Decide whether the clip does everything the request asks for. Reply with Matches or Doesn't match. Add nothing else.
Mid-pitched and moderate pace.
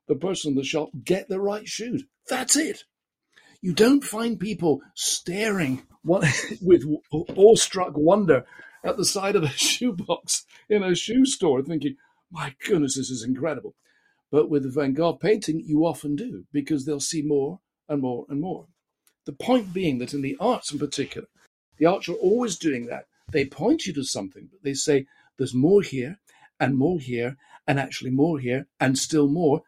Matches